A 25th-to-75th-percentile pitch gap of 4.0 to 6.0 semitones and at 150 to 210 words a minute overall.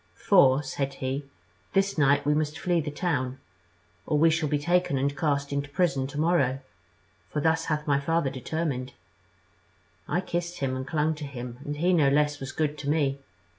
No: average, 2.8 semitones; average, 185 wpm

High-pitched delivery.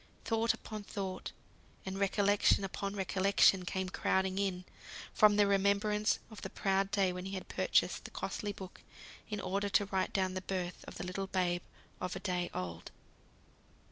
Yes: high, 195 Hz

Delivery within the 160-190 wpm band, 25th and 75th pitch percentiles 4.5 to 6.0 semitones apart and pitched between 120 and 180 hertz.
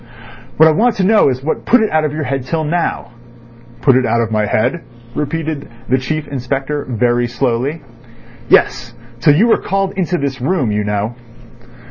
Yes: average, 180 wpm; average, 5.0 semitones; medium, 140 Hz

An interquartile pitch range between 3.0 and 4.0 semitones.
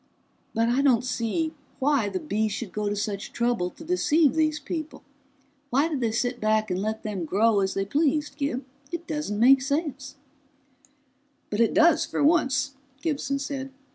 No: wide, 5.5 semitones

